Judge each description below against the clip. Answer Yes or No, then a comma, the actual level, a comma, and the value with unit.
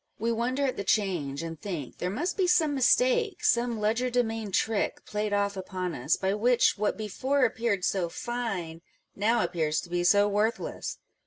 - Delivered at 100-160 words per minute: No, average, 170 wpm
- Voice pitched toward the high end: Yes, high, 210 Hz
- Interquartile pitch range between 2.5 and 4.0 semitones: No, average, 4.8 semitones